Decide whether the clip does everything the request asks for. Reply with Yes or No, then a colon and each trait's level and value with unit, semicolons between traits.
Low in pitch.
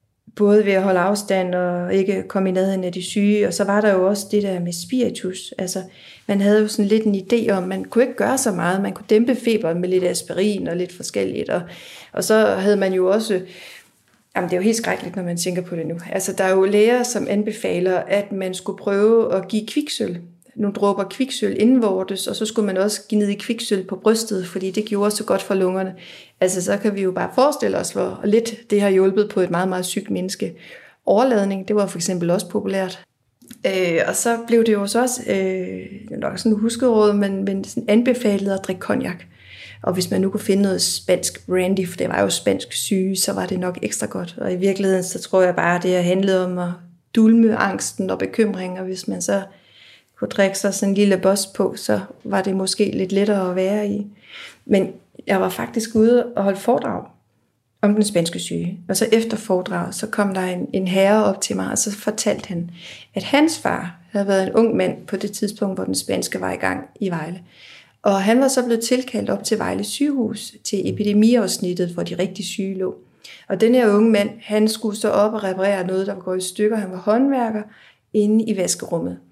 No: high, 200 Hz